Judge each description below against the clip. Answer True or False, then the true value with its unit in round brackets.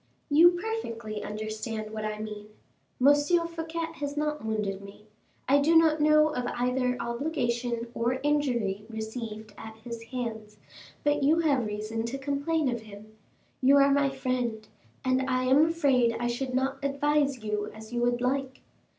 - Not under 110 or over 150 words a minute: False (160 wpm)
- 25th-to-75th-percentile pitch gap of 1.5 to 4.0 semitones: False (4.7 semitones)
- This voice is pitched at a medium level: False (250 Hz)